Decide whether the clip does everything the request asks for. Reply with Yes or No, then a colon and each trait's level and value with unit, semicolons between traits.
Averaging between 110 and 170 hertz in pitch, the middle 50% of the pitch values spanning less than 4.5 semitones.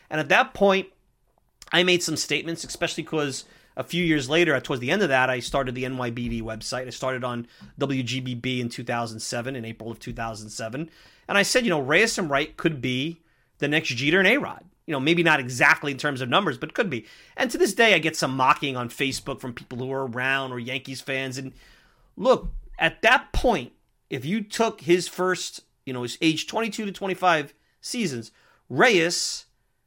No: medium, 140 Hz; average, 5.1 semitones